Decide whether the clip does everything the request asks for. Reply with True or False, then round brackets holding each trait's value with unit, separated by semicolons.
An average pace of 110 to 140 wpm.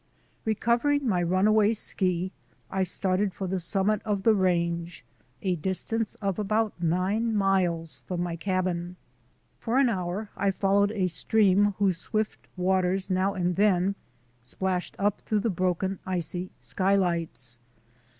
True (135 wpm)